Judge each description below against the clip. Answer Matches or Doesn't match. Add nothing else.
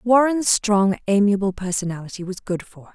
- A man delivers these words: Doesn't match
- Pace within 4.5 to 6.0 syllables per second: Matches